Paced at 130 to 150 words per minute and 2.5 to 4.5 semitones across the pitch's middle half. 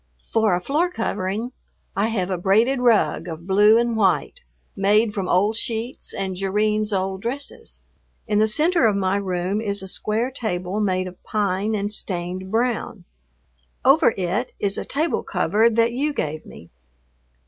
No: average, 160 wpm; average, 3.5 semitones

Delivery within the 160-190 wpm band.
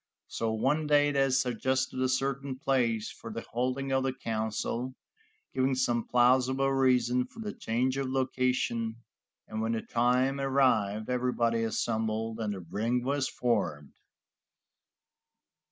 No: slow, 135 wpm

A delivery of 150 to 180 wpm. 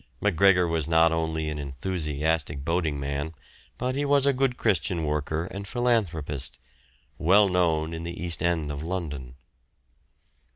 No: average, 140 wpm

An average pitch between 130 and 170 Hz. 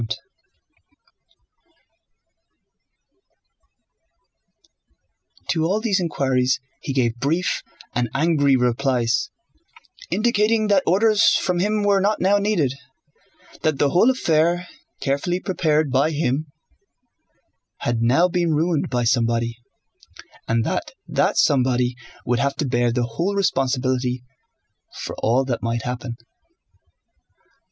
Yes: medium, 140 Hz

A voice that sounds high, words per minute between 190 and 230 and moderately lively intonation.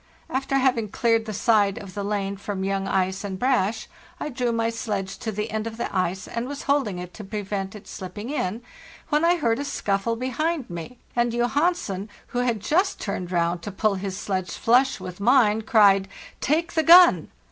Yes: high, 220 Hz; average, 195 wpm; average, 4.4 semitones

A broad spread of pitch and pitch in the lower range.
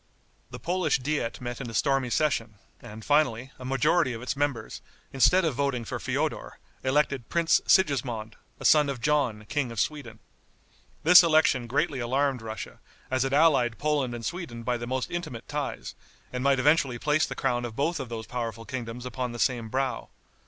No: average, 3.7 semitones; low, 130 Hz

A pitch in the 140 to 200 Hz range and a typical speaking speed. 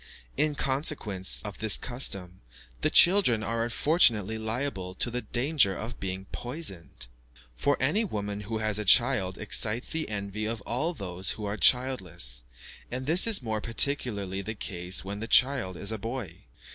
No: low, 110 Hz; average, 160 wpm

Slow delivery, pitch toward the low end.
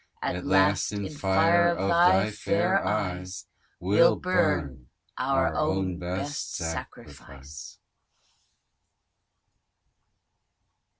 Yes: slow, 75 wpm; low, 100 Hz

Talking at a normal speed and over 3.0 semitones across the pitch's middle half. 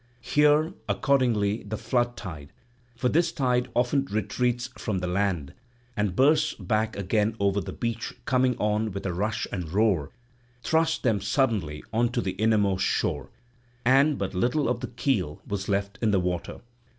Yes: average, 155 wpm; average, 3.9 semitones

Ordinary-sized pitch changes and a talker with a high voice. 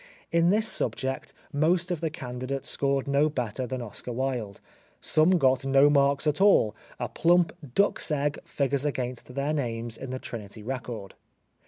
No: average, 3.6 semitones; low, 135 Hz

